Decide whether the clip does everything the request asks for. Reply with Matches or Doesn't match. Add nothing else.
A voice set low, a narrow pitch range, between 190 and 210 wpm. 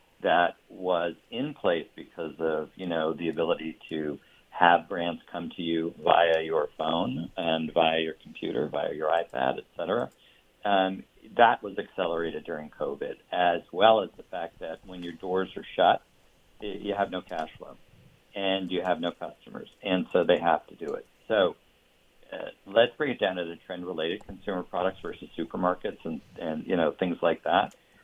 Doesn't match